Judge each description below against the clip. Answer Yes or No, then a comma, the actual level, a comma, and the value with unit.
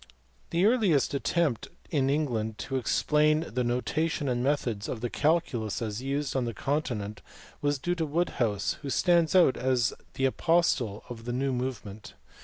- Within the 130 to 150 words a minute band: No, average, 170 wpm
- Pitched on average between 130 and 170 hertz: Yes, low, 135 Hz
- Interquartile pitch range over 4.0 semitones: Yes, average, 4.5 semitones